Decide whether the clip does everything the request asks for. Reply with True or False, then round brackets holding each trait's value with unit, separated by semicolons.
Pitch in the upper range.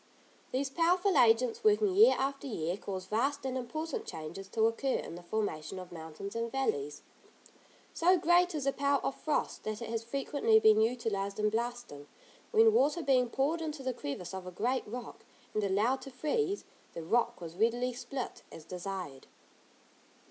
True (240 Hz)